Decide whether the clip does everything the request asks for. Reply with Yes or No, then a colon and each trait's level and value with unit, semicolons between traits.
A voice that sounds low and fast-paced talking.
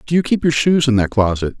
Yes: low, 130 Hz; fast, 300 wpm